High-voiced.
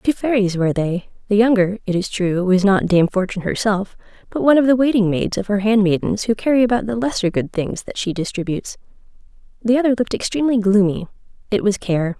Yes: high, 210 Hz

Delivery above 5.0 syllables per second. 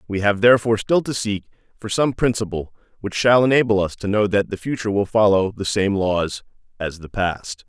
Yes: 5.5 syllables/s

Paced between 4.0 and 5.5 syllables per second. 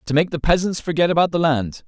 No: 6.2 syllables/s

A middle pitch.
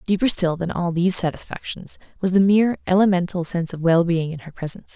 Yes: medium, 175 Hz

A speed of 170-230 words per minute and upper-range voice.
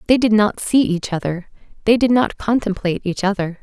Yes: average, 200 wpm; high, 205 Hz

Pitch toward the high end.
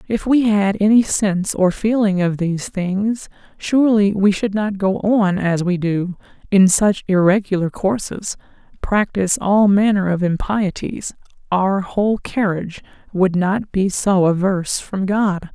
Yes: high, 195 Hz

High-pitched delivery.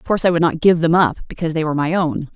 No: medium, 160 Hz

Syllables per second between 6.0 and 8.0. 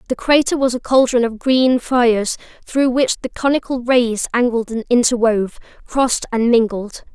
No: 4.9 syllables/s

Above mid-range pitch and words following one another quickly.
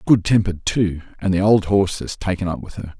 No: very low, 95 Hz; fast, 240 wpm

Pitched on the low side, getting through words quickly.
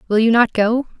No: high, 230 Hz; fast, 240 wpm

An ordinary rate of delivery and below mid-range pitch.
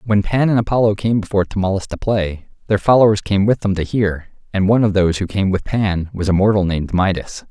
No: fast, 240 wpm; low, 100 Hz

